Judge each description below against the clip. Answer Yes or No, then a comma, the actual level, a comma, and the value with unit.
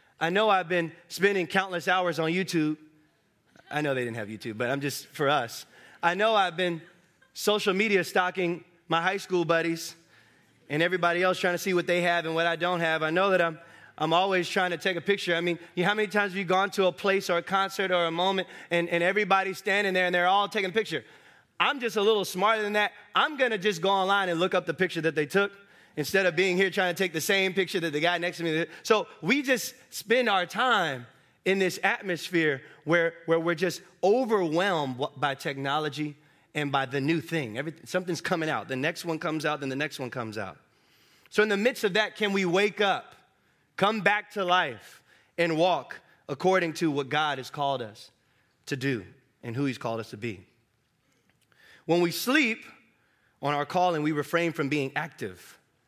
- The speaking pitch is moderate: Yes, medium, 175 Hz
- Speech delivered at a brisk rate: Yes, fast, 220 wpm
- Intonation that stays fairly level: No, average, 4.1 semitones